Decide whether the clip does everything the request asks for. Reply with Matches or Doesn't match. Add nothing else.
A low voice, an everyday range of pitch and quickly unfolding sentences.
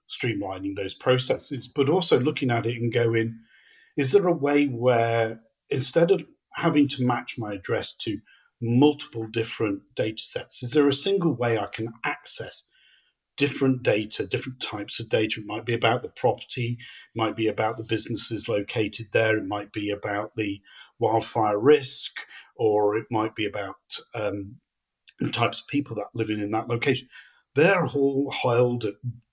Doesn't match